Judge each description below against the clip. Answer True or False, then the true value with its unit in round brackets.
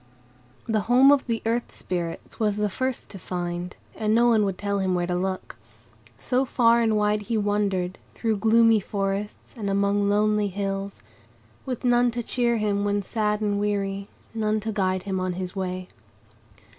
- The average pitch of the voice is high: True (205 Hz)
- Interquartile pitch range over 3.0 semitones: False (2.5 semitones)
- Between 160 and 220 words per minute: True (175 wpm)